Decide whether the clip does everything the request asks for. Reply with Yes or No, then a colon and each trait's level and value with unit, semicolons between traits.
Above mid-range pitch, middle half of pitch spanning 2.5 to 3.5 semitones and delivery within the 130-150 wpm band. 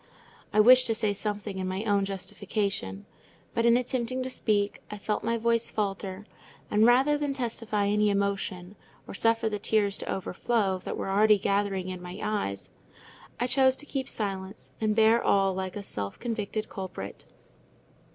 No: high, 210 Hz; average, 2.9 semitones; average, 170 wpm